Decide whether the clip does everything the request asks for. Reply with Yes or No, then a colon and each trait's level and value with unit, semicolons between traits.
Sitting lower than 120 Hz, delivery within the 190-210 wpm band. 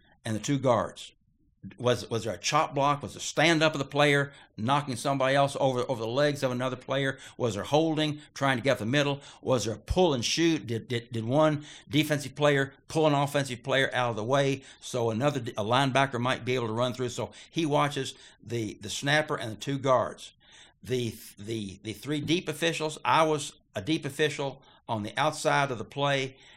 No: low, 135 Hz; fast, 205 wpm